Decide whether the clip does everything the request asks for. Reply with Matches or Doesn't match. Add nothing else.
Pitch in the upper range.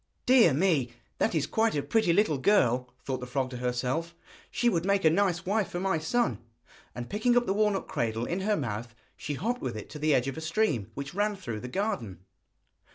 Doesn't match